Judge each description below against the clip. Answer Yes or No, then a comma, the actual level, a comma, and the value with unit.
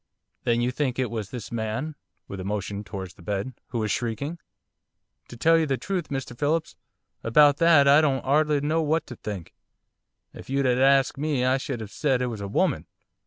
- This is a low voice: Yes, low, 130 Hz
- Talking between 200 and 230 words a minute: Yes, fast, 205 wpm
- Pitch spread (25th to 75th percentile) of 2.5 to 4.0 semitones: No, average, 4.9 semitones